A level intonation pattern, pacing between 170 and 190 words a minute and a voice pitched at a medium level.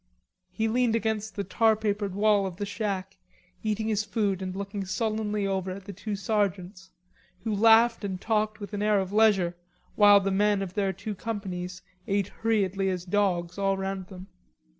No: narrow, 2.1 semitones; average, 180 wpm; high, 200 Hz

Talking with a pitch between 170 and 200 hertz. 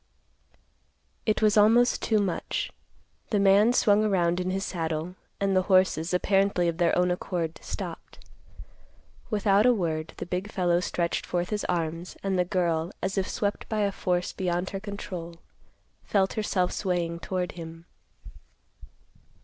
Yes: medium, 185 Hz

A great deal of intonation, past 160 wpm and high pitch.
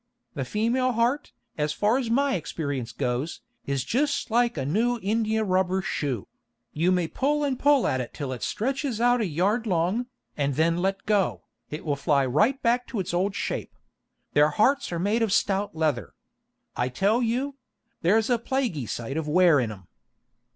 Yes: wide, 7.9 semitones; average, 185 wpm; high, 195 Hz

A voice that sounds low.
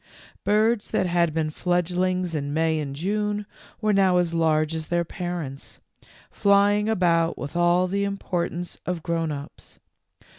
No: medium, 175 Hz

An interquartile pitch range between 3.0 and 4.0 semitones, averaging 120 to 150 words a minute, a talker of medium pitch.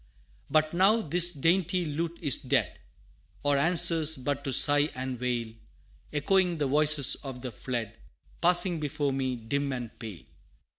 No: average, 4.6 semitones; average, 145 wpm; medium, 145 Hz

